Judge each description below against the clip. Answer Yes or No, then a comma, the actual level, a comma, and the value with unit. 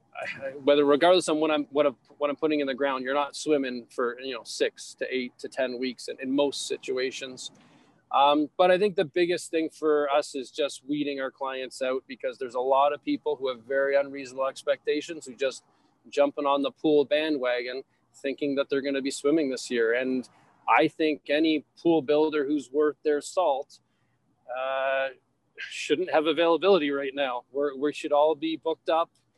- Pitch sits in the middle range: Yes, medium, 145 Hz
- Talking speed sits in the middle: Yes, average, 190 wpm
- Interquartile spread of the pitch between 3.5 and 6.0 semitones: No, narrow, 2.6 semitones